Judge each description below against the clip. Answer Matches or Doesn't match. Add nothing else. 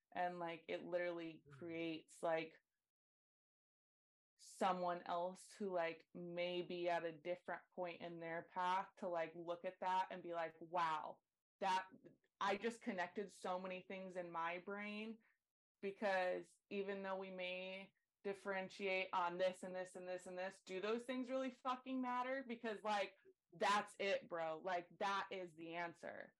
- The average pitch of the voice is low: Doesn't match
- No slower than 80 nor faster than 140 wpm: Doesn't match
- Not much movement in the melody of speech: Matches